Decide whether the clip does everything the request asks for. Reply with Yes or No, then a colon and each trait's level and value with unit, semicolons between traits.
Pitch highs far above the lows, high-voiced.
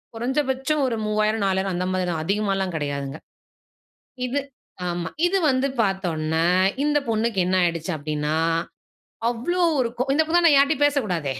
Yes: wide, 7.4 semitones; high, 210 Hz